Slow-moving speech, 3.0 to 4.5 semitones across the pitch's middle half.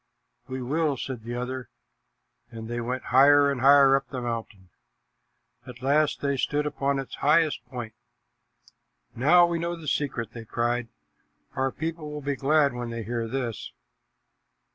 No: average, 155 wpm; average, 3.3 semitones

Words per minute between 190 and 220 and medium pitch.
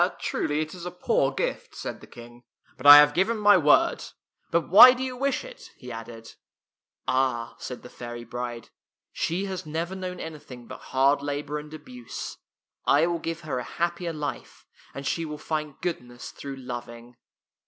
Yes: average, 195 wpm; medium, 150 Hz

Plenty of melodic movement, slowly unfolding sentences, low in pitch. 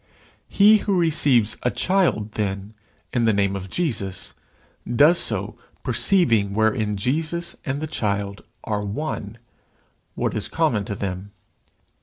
Yes: wide, 7.5 semitones; slow, 130 wpm; low, 110 Hz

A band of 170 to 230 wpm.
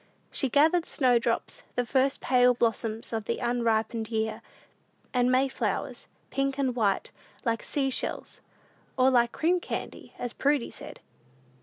No: average, 140 wpm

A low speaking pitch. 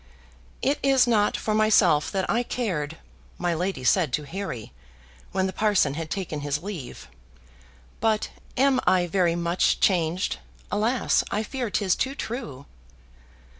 No: high, 190 Hz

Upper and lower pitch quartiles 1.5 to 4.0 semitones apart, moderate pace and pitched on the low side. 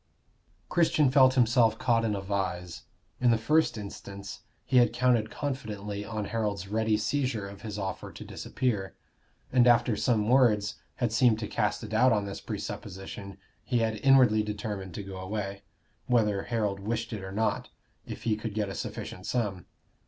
Yes: average, 3.1 semitones; average, 170 wpm; low, 110 Hz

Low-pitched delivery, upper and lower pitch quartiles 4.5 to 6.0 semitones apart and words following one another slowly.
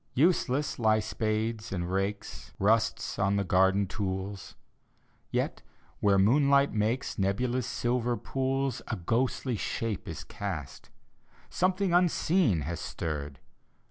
Yes: low, 110 Hz; average, 5.1 semitones; slow, 120 wpm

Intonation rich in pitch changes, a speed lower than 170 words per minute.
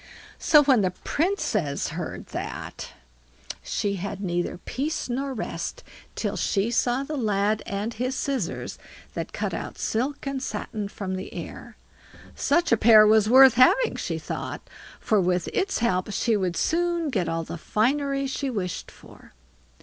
Yes: wide, 5.8 semitones; average, 155 wpm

